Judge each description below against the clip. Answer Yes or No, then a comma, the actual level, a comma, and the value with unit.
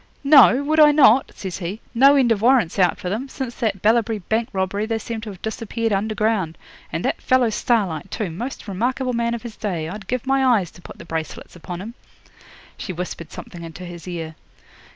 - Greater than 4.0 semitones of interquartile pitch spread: Yes, average, 4.9 semitones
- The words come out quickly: Yes, fast, 210 wpm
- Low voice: No, high, 220 Hz